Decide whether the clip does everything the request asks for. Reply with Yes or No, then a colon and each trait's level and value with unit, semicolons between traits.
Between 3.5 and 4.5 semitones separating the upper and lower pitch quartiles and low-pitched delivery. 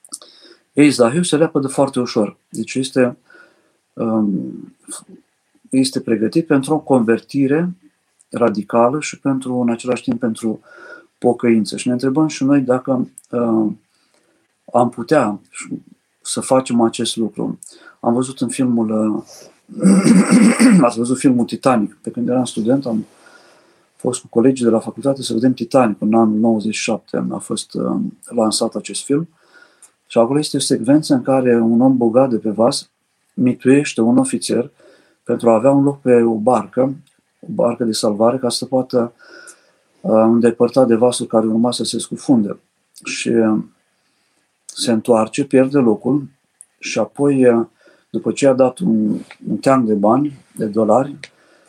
No: average, 3.1 semitones; low, 125 Hz